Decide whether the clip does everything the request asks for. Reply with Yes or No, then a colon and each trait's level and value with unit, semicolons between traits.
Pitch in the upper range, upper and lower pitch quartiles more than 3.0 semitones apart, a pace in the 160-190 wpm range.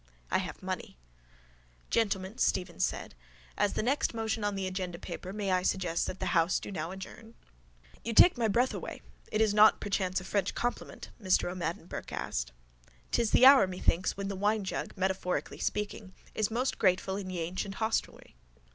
No: high, 195 Hz; average, 2.7 semitones; average, 175 wpm